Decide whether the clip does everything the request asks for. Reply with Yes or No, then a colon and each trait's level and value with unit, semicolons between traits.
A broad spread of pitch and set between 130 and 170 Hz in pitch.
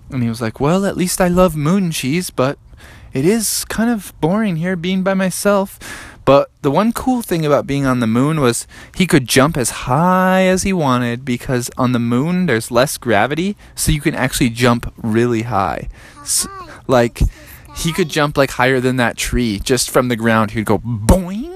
Yes: wide, 7.3 semitones; medium, 140 Hz